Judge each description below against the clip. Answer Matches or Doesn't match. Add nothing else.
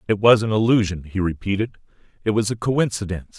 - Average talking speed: Matches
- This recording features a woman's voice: Doesn't match